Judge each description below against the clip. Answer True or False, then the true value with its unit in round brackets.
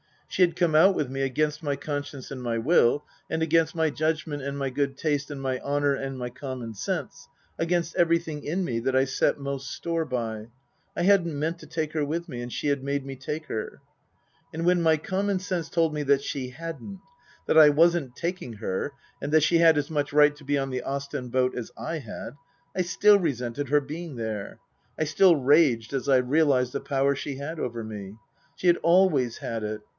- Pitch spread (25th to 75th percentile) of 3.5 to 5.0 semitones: True (3.9 semitones)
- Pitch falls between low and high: True (145 Hz)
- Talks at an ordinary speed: False (215 wpm)